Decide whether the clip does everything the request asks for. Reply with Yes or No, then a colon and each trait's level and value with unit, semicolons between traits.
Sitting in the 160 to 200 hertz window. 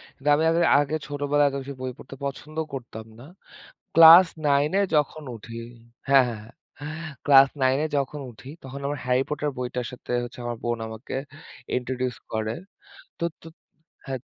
No: low, 135 Hz